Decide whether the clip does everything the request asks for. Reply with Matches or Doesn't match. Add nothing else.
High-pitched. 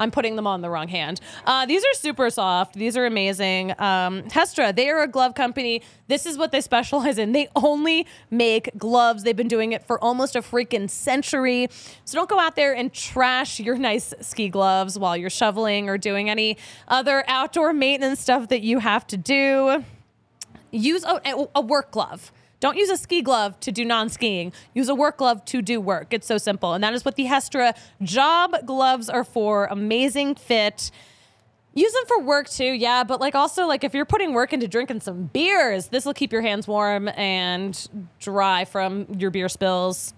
Matches